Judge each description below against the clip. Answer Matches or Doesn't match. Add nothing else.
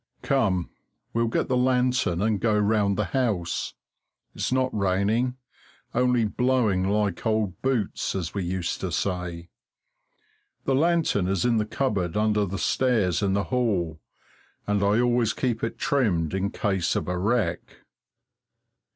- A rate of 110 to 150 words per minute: Matches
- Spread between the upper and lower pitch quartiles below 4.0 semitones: Doesn't match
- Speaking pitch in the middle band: Doesn't match